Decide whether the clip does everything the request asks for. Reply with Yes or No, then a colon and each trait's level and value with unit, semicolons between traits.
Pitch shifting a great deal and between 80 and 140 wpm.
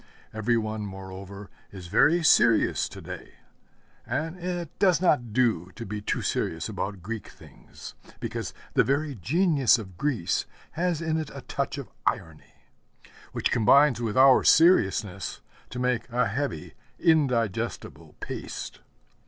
Yes: wide, 6.5 semitones; slow, 135 wpm